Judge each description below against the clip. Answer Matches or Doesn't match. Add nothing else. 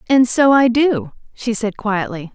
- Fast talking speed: Doesn't match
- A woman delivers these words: Matches